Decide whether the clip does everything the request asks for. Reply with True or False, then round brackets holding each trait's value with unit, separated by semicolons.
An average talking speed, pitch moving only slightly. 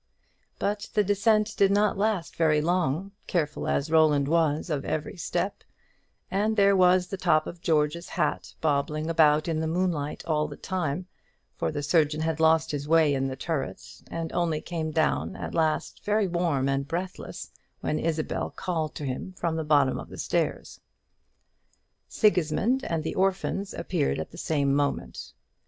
False (165 wpm; 3.4 semitones)